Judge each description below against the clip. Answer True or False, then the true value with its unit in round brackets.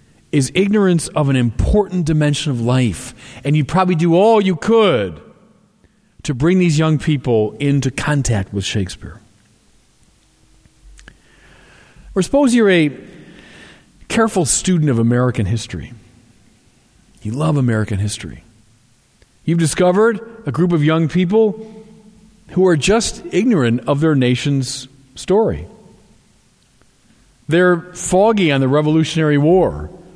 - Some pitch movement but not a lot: False (7.3 semitones)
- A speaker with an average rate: False (115 wpm)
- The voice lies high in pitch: False (145 Hz)